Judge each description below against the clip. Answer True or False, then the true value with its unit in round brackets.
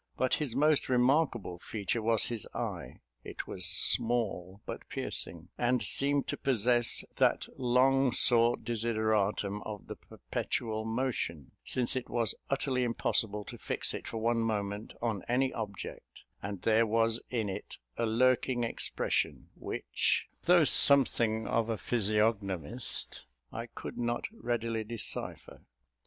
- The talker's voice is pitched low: True (115 Hz)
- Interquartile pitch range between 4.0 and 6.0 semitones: False (2.6 semitones)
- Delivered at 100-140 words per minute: True (135 wpm)